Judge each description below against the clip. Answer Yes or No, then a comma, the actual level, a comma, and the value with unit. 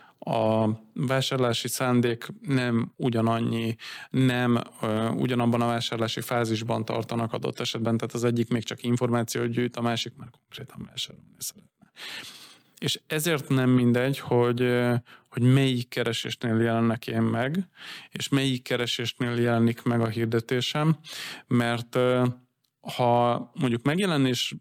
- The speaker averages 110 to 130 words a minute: Yes, average, 115 wpm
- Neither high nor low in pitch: No, low, 120 Hz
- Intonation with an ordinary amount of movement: No, narrow, 1.8 semitones